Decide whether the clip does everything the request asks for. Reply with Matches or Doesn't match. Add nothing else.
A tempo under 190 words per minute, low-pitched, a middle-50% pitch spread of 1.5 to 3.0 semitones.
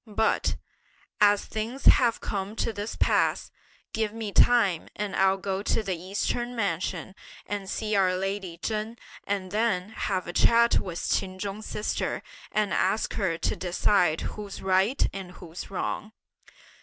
Doesn't match